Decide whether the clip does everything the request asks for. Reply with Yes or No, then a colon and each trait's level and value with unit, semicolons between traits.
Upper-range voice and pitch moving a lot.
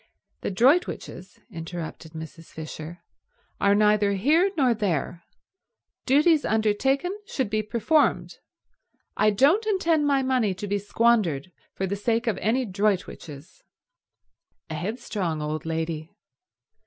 Yes: high, 210 Hz; wide, 7.3 semitones